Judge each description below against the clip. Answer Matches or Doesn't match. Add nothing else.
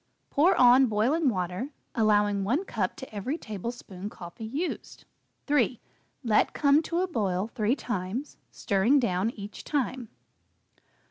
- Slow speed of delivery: Matches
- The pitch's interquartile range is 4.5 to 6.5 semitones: Matches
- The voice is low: Doesn't match